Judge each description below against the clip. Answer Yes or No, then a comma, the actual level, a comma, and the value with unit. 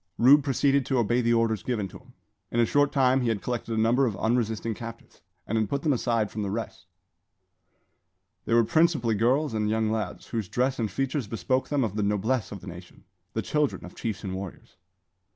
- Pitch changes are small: No, average, 3.3 semitones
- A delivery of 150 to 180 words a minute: No, fast, 205 wpm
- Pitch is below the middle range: Yes, low, 115 Hz